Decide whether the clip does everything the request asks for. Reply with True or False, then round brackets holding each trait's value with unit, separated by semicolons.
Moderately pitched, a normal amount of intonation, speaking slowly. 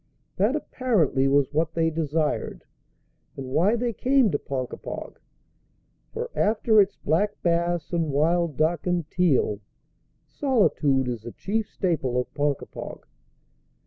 False (165 Hz; 6.1 semitones; 125 wpm)